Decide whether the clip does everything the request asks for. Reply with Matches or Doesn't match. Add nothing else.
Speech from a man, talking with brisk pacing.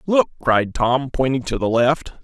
Doesn't match